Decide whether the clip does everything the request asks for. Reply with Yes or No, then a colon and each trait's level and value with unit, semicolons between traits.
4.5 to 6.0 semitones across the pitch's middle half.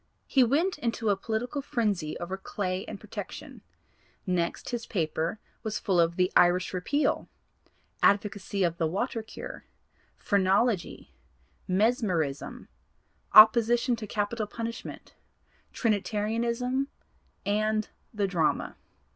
No: average, 4.1 semitones